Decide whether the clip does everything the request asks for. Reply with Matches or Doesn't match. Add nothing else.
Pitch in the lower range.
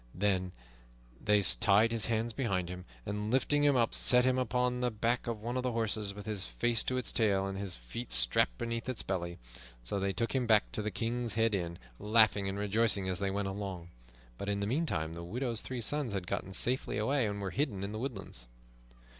Matches